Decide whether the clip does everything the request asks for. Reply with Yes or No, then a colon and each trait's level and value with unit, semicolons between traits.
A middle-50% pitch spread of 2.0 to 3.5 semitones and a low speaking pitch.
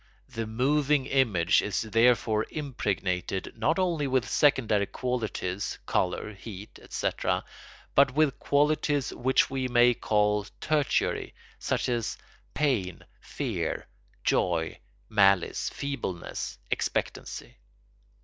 No: wide, 5.4 semitones; low, 120 Hz